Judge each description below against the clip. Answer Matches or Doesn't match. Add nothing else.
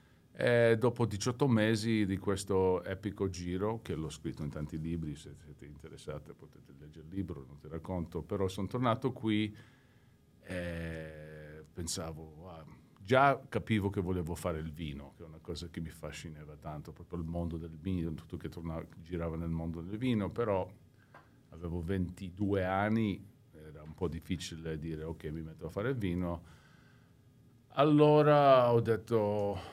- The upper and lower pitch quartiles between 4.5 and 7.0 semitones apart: Matches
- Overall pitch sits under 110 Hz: Matches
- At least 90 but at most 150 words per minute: Doesn't match